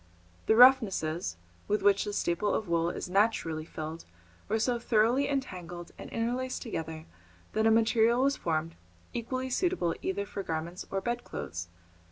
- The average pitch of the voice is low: No, high, 205 Hz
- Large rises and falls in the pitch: Yes, wide, 6.0 semitones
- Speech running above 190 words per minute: No, average, 150 wpm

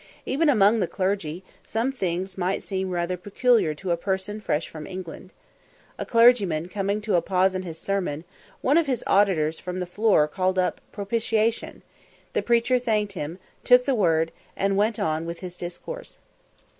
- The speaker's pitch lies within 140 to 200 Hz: Yes, high, 190 Hz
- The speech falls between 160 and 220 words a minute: Yes, average, 170 wpm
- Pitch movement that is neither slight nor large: Yes, average, 4.0 semitones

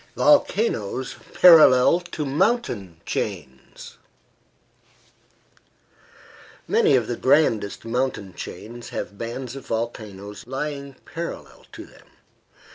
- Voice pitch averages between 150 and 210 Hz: No, low, 125 Hz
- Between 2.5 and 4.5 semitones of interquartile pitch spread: No, wide, 5.4 semitones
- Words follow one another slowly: Yes, slow, 90 wpm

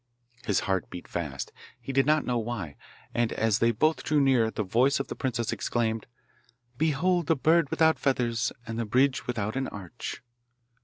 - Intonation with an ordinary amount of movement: Yes, average, 3.9 semitones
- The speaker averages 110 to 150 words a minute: No, average, 175 wpm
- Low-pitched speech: Yes, low, 120 Hz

